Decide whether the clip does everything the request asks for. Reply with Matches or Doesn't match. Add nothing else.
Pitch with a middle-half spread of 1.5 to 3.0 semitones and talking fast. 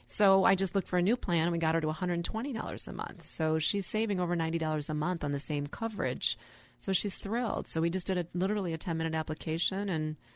Doesn't match